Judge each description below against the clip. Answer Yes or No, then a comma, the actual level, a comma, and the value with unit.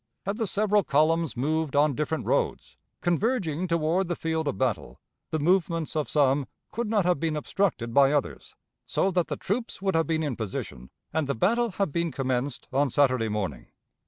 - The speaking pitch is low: No, medium, 160 Hz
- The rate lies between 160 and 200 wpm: Yes, average, 185 wpm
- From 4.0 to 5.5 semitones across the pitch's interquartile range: Yes, average, 4.8 semitones